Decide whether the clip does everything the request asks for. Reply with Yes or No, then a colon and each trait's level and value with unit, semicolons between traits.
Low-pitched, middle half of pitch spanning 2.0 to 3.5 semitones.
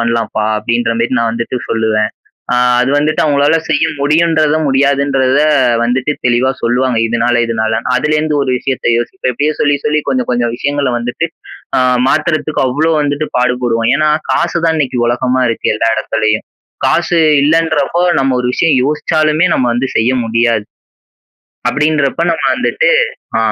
No: low, 130 Hz; average, 4.2 semitones